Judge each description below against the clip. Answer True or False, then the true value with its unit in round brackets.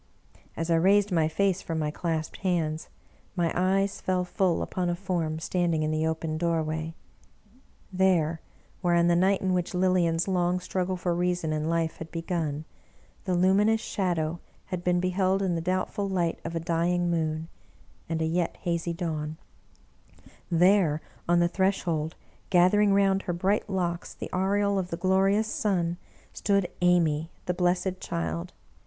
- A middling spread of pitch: False (2.3 semitones)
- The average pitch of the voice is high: False (175 Hz)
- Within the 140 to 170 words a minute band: True (160 wpm)